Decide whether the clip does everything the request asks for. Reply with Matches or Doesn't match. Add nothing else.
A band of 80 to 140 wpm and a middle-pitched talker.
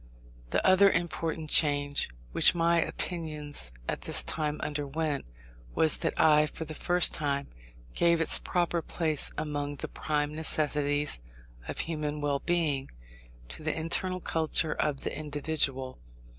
Matches